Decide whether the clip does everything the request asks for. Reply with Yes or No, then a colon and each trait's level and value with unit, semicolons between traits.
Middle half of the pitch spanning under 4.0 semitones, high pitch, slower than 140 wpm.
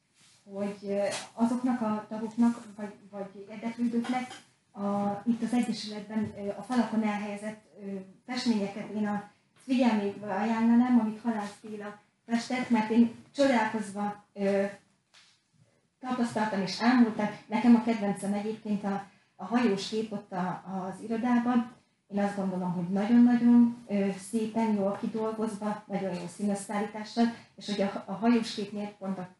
Yes: narrow, 2.5 semitones; high, 210 Hz; average, 120 wpm